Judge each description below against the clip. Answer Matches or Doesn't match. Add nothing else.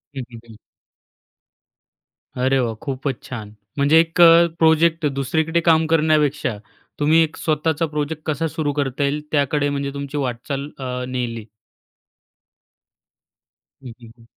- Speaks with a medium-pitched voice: Matches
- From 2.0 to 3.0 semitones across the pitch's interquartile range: Doesn't match